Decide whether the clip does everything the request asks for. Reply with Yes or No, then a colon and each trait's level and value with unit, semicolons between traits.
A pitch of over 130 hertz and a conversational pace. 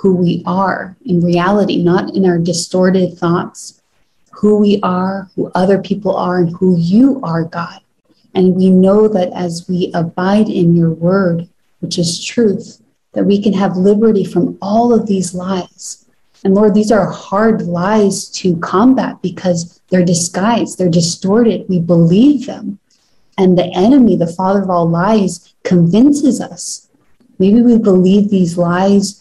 Yes: high, 190 Hz; average, 155 wpm